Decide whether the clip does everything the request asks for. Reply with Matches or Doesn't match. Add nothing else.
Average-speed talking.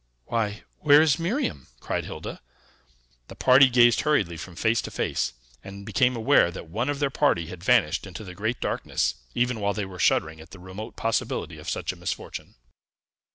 Matches